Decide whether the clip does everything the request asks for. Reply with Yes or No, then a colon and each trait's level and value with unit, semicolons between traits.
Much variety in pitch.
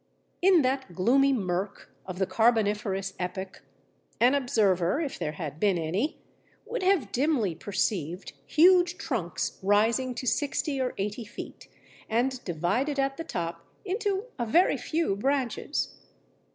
Yes: wide, 6.9 semitones